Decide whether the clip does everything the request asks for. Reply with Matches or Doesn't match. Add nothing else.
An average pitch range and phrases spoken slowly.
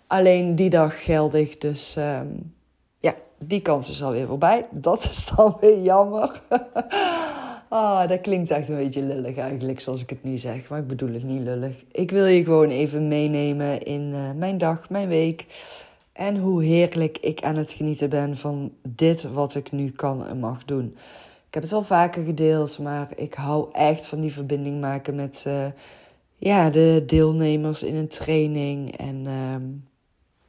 Doesn't match